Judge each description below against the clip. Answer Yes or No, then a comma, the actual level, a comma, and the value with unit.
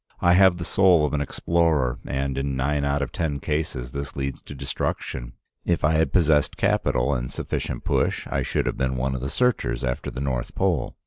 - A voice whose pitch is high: No, very low, 70 Hz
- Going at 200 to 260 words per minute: Yes, fast, 205 wpm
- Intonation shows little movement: No, average, 3.4 semitones